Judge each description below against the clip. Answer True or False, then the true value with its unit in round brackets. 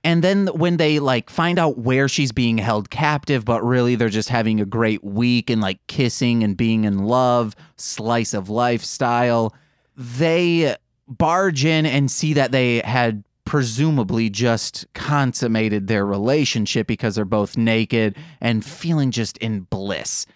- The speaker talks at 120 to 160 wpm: True (155 wpm)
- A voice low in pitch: True (120 Hz)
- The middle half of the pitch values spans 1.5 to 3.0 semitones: False (4.3 semitones)